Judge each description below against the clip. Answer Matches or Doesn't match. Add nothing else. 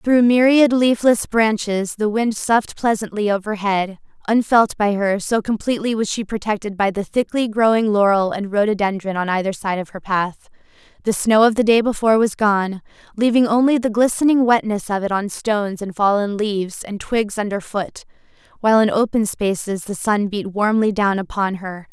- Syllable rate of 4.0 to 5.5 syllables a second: Matches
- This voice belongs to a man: Doesn't match